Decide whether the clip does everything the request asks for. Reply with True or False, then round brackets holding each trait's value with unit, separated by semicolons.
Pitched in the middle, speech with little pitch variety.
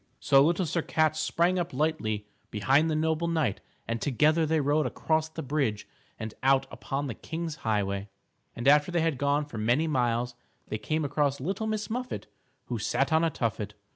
False (150 Hz; 4.7 semitones)